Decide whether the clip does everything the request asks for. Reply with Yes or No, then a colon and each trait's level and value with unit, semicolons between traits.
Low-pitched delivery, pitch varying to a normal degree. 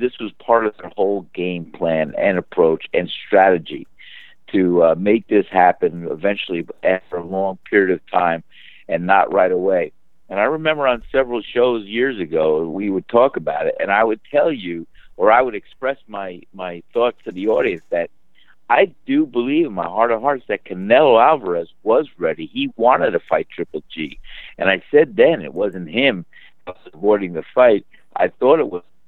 No: low, 105 Hz; wide, 7.0 semitones